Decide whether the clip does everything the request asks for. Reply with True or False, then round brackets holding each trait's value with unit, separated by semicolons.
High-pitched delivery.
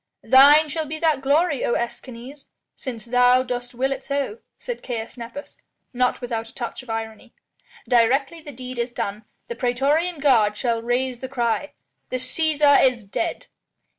True (255 Hz)